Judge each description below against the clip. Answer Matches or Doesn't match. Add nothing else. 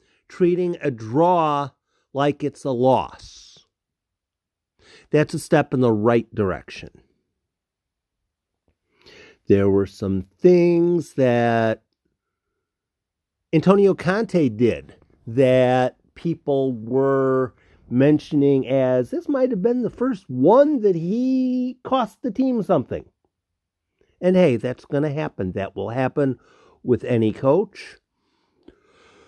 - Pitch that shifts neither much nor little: Doesn't match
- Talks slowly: Matches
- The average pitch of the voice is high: Doesn't match